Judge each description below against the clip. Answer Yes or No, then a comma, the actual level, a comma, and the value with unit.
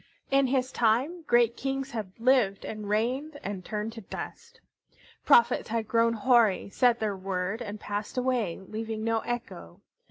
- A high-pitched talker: Yes, high, 230 Hz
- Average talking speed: Yes, average, 155 wpm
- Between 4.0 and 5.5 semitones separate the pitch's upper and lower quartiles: No, average, 3.3 semitones